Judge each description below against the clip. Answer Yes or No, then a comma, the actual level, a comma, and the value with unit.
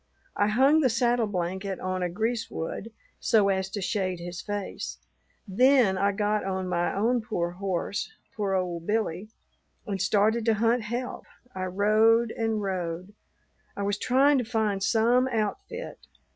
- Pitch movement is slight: No, average, 3.4 semitones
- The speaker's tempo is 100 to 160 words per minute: Yes, average, 150 wpm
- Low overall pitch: No, high, 205 Hz